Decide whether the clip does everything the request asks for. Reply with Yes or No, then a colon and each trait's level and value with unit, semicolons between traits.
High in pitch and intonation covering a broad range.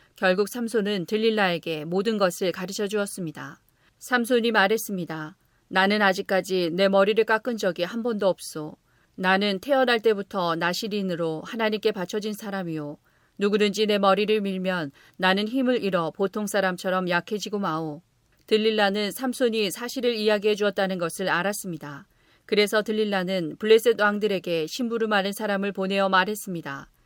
No: high, 200 Hz; average, 2.9 semitones